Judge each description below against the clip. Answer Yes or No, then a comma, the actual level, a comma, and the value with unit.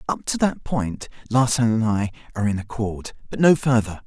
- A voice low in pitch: Yes, low, 115 Hz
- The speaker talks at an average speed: Yes, average, 190 wpm